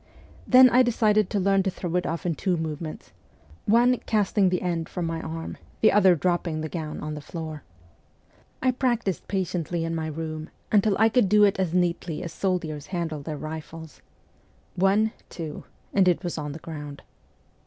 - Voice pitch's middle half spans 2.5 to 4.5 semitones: Yes, average, 3.8 semitones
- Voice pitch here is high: No, medium, 175 Hz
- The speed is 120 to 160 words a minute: No, average, 185 wpm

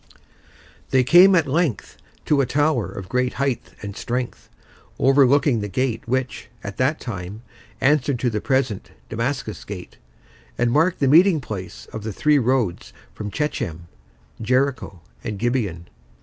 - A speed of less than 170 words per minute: Yes, average, 145 wpm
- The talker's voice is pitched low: Yes, low, 125 Hz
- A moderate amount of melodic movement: Yes, average, 4.9 semitones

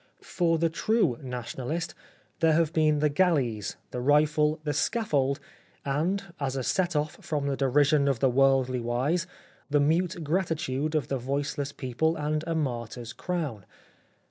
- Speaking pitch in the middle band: Yes, medium, 145 Hz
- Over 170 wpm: No, average, 155 wpm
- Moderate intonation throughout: Yes, average, 3.5 semitones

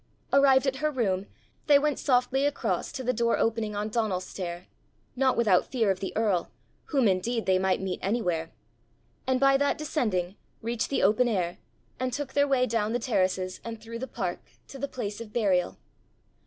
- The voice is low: No, high, 230 Hz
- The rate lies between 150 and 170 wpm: No, average, 185 wpm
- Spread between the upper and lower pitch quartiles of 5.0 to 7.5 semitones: Yes, wide, 5.4 semitones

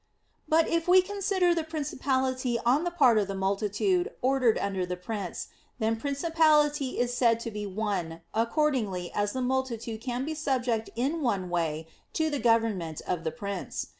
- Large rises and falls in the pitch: Yes, wide, 6.5 semitones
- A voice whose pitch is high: Yes, high, 245 Hz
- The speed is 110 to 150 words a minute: No, average, 165 wpm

